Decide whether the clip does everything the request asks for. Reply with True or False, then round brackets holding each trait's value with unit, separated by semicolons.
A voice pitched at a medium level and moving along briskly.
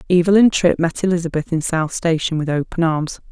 False (170 Hz; 180 wpm)